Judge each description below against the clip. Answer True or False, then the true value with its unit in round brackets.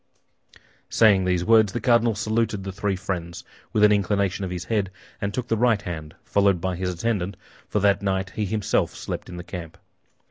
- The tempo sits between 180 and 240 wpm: True (190 wpm)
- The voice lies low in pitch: True (100 Hz)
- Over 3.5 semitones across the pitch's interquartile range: False (2.8 semitones)